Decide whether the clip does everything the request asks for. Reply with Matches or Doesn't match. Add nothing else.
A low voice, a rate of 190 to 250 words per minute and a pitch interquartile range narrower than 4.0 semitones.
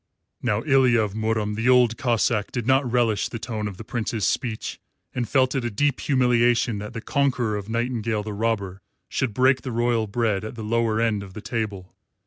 Matches